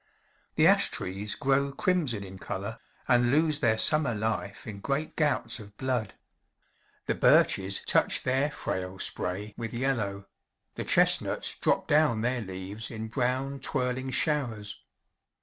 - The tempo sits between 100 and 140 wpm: Yes, slow, 135 wpm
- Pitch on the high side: No, low, 120 Hz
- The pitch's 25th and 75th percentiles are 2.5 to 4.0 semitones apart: No, average, 4.9 semitones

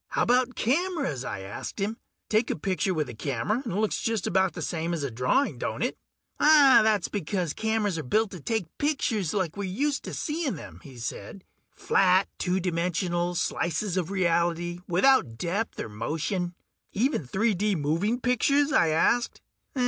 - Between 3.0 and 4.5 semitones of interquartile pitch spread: No, average, 5.2 semitones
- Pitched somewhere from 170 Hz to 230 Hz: Yes, high, 190 Hz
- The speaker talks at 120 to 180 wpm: Yes, average, 170 wpm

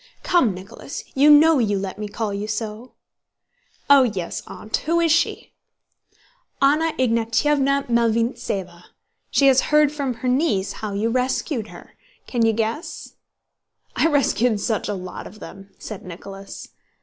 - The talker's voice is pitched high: Yes, high, 230 Hz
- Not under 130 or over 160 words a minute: Yes, average, 145 wpm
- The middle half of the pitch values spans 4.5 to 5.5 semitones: Yes, average, 5.2 semitones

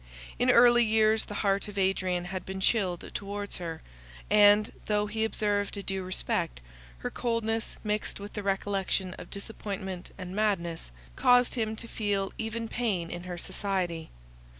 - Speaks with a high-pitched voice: Yes, high, 200 Hz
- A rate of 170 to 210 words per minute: No, average, 155 wpm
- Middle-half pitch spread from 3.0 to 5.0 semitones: No, narrow, 2.6 semitones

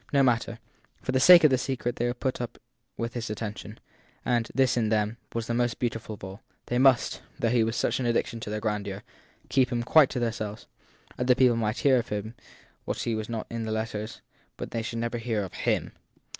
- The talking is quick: Yes, fast, 210 wpm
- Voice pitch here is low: Yes, low, 115 Hz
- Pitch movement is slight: Yes, narrow, 2.1 semitones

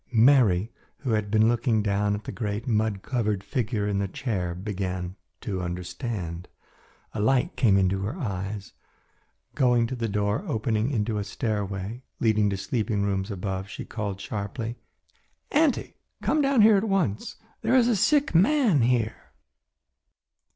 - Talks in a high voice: No, low, 110 Hz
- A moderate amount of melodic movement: Yes, average, 4.1 semitones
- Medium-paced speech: Yes, average, 150 wpm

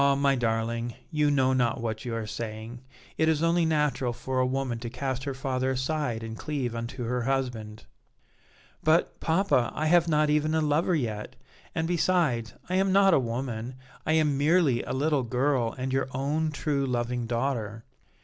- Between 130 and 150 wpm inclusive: No, average, 180 wpm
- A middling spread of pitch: Yes, average, 4.4 semitones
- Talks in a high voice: No, low, 130 Hz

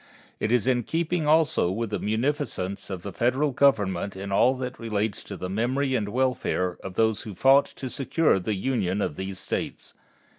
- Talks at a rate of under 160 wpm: No, average, 190 wpm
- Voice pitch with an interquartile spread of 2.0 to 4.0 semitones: No, average, 5.2 semitones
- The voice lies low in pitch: Yes, low, 115 Hz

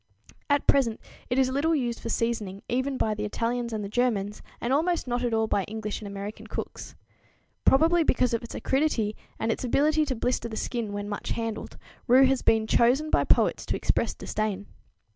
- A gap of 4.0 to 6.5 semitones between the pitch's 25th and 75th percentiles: No, average, 3.6 semitones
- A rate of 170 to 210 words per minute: Yes, average, 195 wpm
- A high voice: Yes, high, 235 Hz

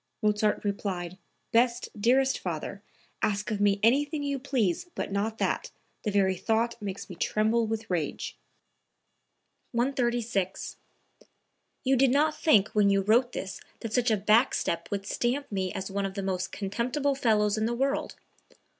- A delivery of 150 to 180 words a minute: Yes, average, 155 wpm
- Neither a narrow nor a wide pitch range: Yes, average, 3.7 semitones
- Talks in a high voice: Yes, high, 215 Hz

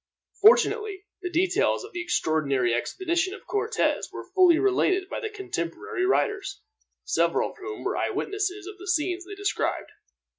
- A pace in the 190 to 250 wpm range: No, average, 145 wpm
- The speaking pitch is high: Yes, very high, 380 Hz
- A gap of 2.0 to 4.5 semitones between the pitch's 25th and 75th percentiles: Yes, narrow, 2.6 semitones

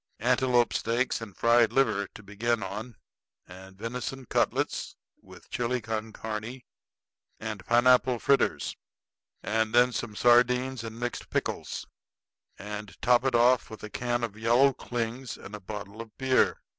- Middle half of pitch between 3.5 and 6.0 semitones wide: No, narrow, 2.5 semitones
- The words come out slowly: No, average, 145 wpm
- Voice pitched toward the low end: Yes, low, 115 Hz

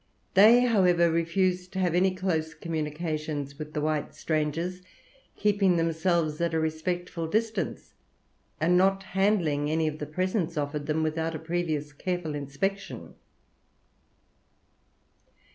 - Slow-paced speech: Yes, slow, 125 wpm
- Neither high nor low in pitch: Yes, medium, 165 Hz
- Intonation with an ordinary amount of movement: Yes, average, 3.1 semitones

